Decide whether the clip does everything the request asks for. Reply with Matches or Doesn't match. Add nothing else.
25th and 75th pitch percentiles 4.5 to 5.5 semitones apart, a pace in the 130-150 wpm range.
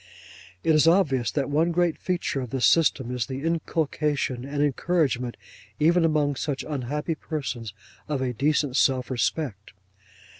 Doesn't match